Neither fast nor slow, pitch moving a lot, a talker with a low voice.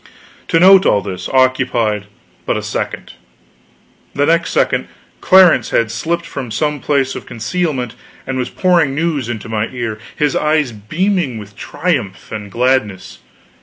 Yes: average, 145 wpm; wide, 6.5 semitones; low, 130 Hz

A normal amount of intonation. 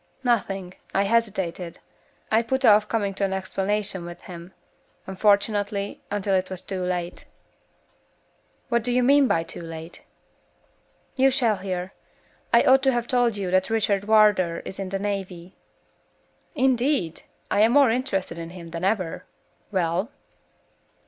Yes: average, 3.8 semitones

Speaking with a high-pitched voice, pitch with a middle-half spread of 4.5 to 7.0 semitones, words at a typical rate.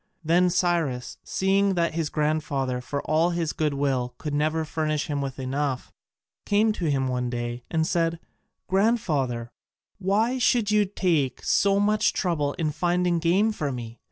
No: medium, 160 Hz; average, 4.9 semitones; average, 155 wpm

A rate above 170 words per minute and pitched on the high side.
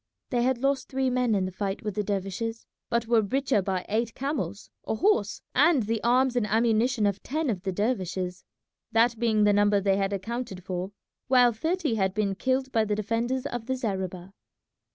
Yes: average, 195 wpm; high, 225 Hz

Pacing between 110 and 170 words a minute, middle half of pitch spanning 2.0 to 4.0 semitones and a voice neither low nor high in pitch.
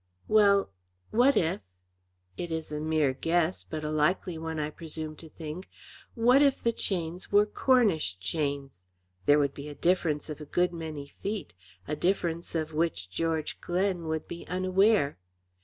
Yes: average, 160 wpm; average, 3.5 semitones; medium, 165 Hz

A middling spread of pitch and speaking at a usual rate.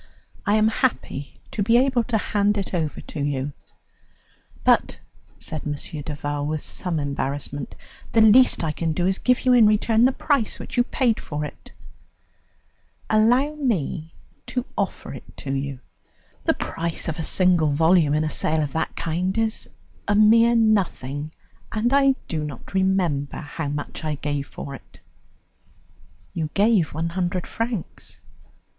No: wide, 6.8 semitones; average, 160 wpm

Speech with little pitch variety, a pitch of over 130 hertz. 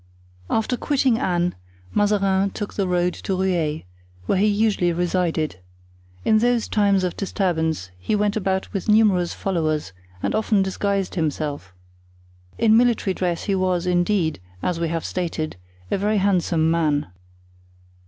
No: average, 3.6 semitones; medium, 185 Hz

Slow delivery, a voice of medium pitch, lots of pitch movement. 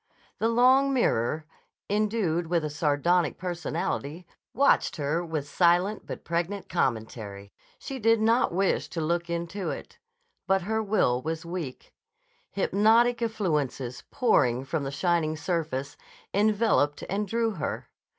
Yes: slow, 130 wpm; medium, 175 Hz; wide, 6.1 semitones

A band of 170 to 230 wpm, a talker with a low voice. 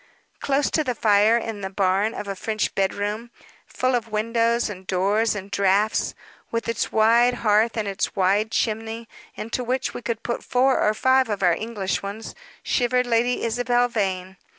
No: average, 175 wpm; high, 220 Hz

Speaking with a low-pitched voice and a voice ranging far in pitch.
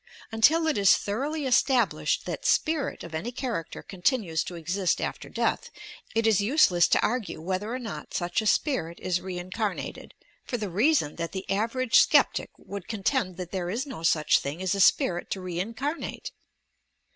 No: high, 200 Hz; wide, 5.8 semitones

